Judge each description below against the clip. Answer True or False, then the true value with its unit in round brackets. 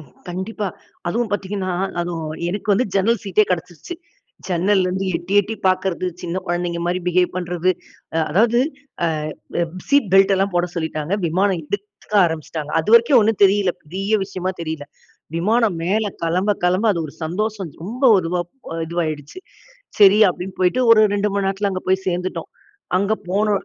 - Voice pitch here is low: False (185 Hz)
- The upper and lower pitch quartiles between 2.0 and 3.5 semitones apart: True (2.9 semitones)